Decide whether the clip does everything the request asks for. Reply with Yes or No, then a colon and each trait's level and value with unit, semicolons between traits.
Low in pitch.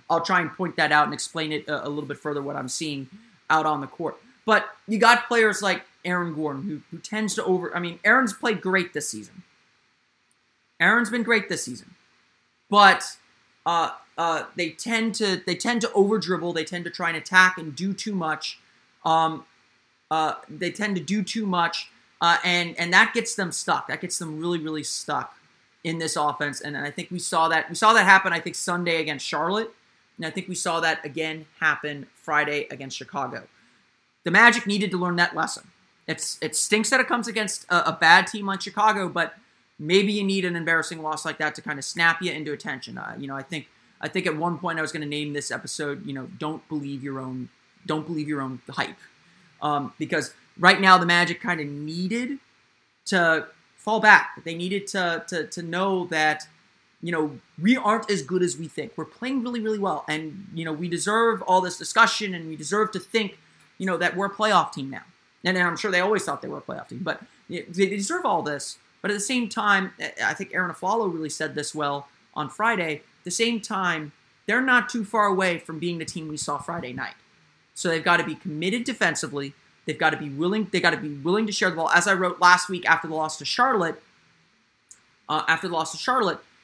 No: medium, 175 Hz